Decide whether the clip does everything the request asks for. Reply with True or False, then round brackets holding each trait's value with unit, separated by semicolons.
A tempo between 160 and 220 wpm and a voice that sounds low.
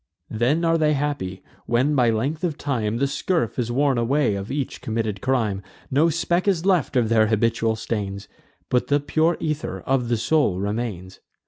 True (180 wpm; 125 Hz)